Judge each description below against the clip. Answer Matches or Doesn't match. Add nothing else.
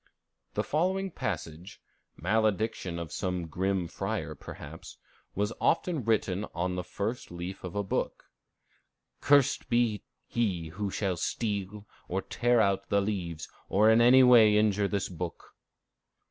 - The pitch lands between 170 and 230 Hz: Doesn't match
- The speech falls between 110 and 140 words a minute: Matches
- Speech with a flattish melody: Doesn't match